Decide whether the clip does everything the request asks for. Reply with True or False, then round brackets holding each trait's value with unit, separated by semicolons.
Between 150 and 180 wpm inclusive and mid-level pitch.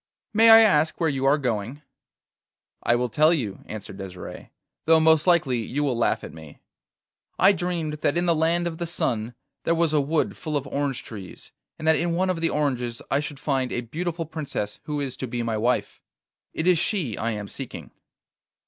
False (200 wpm; 145 Hz)